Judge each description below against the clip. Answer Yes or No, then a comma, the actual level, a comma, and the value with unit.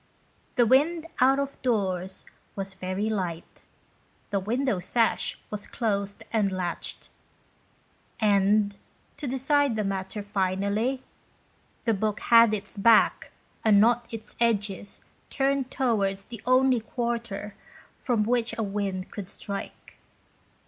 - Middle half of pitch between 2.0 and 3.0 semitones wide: No, average, 3.5 semitones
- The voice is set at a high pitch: Yes, high, 215 Hz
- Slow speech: Yes, slow, 120 wpm